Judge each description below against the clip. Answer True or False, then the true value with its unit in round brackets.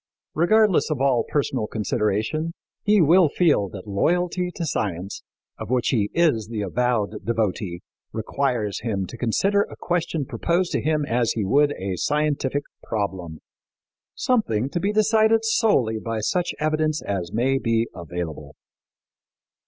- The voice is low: True (125 Hz)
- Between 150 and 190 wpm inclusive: False (140 wpm)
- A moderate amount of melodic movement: False (7.8 semitones)